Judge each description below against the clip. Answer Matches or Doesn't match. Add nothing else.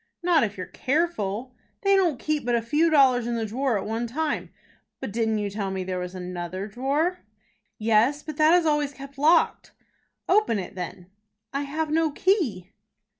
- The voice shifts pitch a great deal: Matches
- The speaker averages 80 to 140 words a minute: Doesn't match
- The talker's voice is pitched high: Matches